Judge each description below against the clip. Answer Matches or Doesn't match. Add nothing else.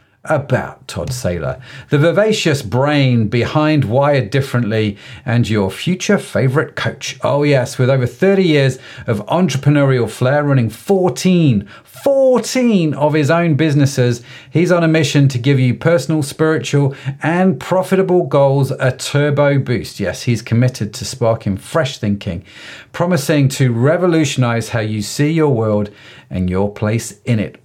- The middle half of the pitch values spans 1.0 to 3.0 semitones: Doesn't match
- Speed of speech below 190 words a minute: Matches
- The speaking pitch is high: Doesn't match